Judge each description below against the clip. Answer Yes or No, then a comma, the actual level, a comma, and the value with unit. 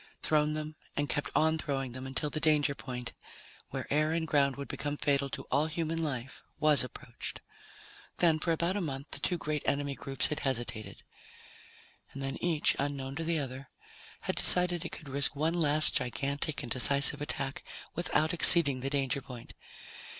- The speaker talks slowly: No, average, 170 wpm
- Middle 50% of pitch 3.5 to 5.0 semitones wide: No, narrow, 2.5 semitones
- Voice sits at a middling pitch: Yes, medium, 145 Hz